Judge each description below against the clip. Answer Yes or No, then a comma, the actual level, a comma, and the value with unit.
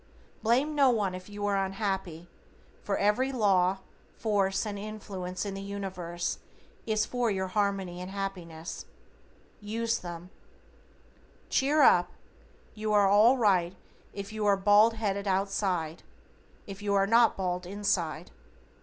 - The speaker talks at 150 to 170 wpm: No, slow, 135 wpm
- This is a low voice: No, high, 200 Hz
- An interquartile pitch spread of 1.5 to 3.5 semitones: Yes, narrow, 2.5 semitones